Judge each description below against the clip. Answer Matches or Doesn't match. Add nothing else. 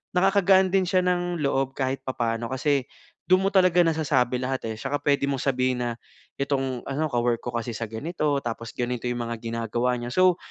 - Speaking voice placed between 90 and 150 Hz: Matches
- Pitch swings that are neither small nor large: Doesn't match